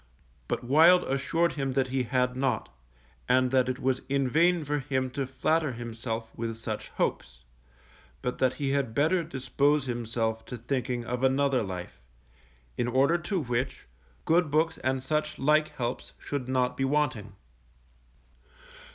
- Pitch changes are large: No, average, 2.9 semitones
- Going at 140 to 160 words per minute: Yes, average, 150 wpm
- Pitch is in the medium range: No, low, 130 Hz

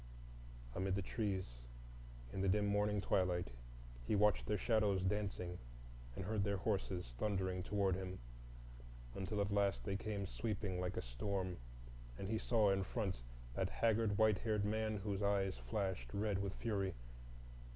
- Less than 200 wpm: Yes, average, 150 wpm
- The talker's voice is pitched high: No, low, 100 Hz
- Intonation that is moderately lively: No, narrow, 1.9 semitones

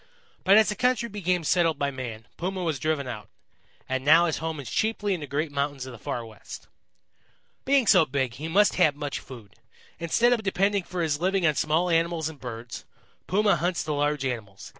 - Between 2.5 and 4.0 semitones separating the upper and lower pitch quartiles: No, average, 5.2 semitones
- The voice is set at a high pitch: No, medium, 160 Hz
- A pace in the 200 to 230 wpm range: Yes, fast, 205 wpm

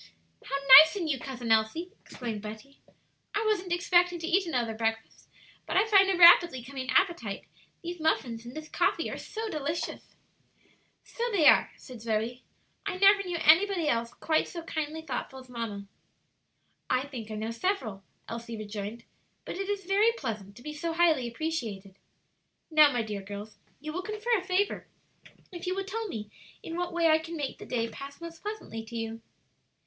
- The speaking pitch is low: No, very high, 300 Hz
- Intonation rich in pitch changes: Yes, wide, 7.5 semitones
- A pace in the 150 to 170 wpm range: No, average, 180 wpm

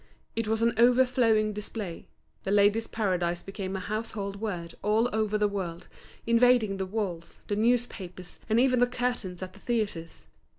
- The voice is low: No, high, 210 Hz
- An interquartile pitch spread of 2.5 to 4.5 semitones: Yes, average, 3.2 semitones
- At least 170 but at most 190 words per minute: No, average, 160 wpm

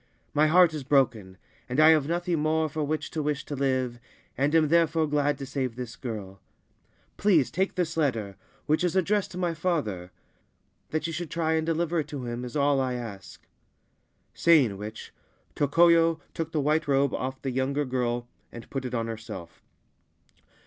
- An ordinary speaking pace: Yes, average, 180 wpm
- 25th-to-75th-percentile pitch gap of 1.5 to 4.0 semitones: No, average, 4.5 semitones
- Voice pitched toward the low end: No, medium, 145 Hz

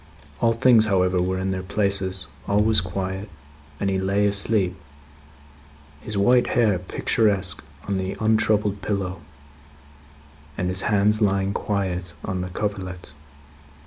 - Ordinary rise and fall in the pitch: No, narrow, 2.1 semitones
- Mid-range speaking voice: No, low, 100 Hz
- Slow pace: Yes, slow, 130 wpm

